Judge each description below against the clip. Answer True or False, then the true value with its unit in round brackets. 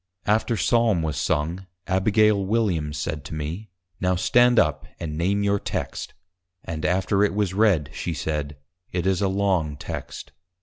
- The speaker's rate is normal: True (160 wpm)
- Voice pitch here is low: True (95 Hz)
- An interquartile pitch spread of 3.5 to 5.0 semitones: True (4.6 semitones)